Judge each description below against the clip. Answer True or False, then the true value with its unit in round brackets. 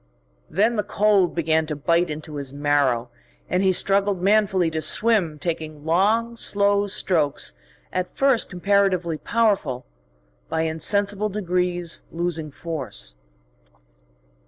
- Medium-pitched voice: True (175 Hz)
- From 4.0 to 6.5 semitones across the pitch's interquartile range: True (4.5 semitones)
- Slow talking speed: True (115 wpm)